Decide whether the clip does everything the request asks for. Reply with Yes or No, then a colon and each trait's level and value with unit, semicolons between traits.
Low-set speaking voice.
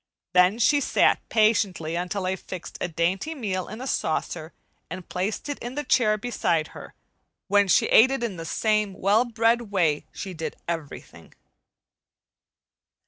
No: high, 200 Hz